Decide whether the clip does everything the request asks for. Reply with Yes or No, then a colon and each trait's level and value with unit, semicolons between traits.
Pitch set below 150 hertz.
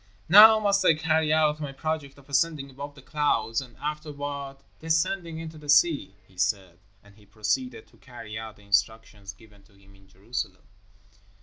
Yes: low, 135 Hz